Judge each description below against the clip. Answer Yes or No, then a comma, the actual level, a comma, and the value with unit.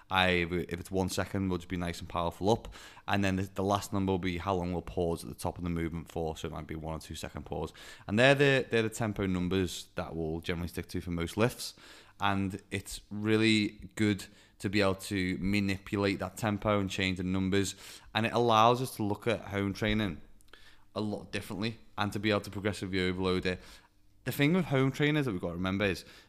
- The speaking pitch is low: Yes, low, 100 Hz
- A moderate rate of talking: No, fast, 230 wpm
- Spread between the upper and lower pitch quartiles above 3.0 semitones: No, average, 2.7 semitones